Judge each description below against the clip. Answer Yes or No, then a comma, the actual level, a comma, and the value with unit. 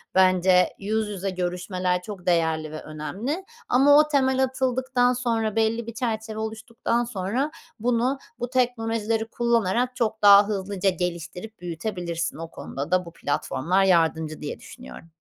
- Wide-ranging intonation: No, average, 4.9 semitones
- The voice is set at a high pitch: Yes, high, 210 Hz